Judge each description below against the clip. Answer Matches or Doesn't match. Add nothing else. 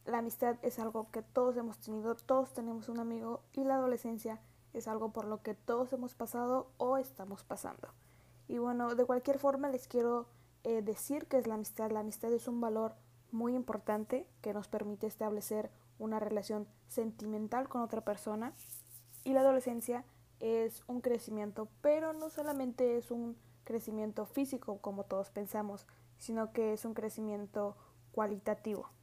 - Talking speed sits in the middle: Matches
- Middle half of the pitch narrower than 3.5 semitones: Matches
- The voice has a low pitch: Doesn't match